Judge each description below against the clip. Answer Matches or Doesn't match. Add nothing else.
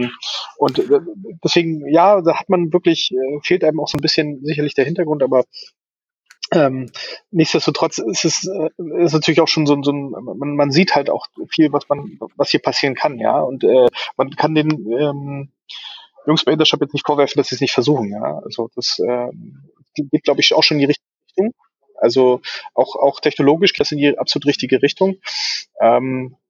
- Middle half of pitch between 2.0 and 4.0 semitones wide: Matches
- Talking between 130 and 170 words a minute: Doesn't match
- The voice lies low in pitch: Doesn't match